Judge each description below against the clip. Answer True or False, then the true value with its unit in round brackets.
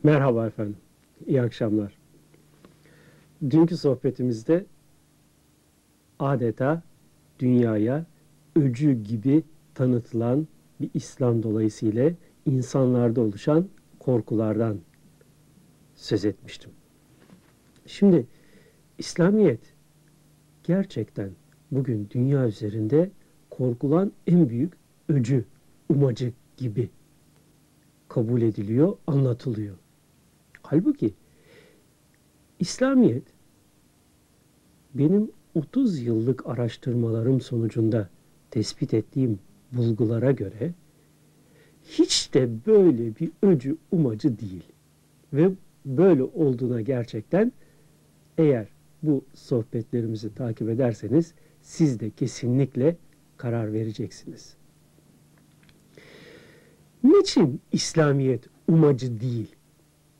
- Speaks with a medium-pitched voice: False (130 Hz)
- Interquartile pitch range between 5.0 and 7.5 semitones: True (5.3 semitones)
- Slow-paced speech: True (70 wpm)